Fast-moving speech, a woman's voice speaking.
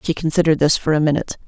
Yes: fast, 245 wpm; female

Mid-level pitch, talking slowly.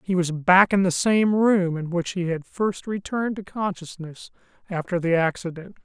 No: medium, 180 Hz; average, 185 wpm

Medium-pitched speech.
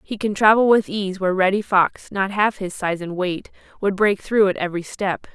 No: high, 195 Hz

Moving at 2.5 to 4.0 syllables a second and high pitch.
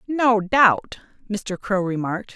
Yes: 3.9 syllables/s; high, 210 Hz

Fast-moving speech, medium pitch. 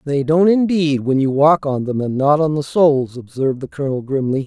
Yes: fast, 230 wpm; medium, 145 Hz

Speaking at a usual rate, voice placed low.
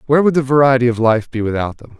No: fast, 270 wpm; low, 125 Hz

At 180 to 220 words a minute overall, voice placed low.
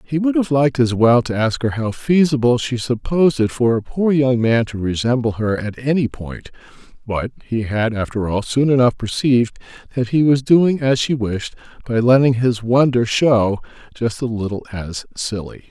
Yes: average, 190 wpm; low, 125 Hz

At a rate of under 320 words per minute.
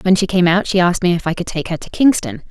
No: fast, 335 wpm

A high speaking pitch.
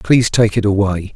No: low, 105 Hz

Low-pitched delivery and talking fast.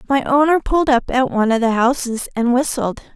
No: very high, 255 Hz; fast, 210 wpm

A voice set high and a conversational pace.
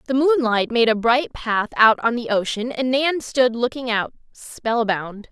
Yes: high, 240 Hz; average, 180 wpm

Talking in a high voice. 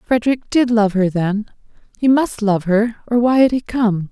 Yes: high, 225 Hz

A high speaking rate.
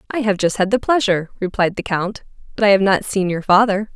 Yes: fast, 245 wpm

